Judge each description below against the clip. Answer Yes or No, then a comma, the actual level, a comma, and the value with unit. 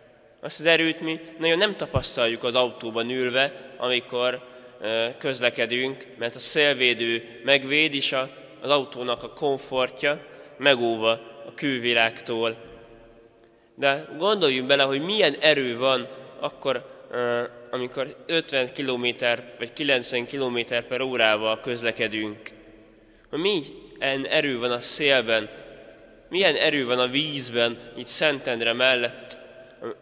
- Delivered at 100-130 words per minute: Yes, average, 110 wpm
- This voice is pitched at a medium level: No, low, 125 Hz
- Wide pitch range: No, average, 2.9 semitones